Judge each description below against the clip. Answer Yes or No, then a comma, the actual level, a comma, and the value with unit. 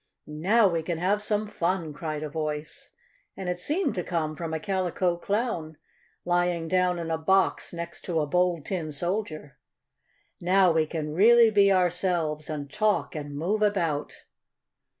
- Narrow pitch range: No, average, 3.4 semitones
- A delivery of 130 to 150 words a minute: No, average, 160 wpm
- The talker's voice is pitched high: No, medium, 175 Hz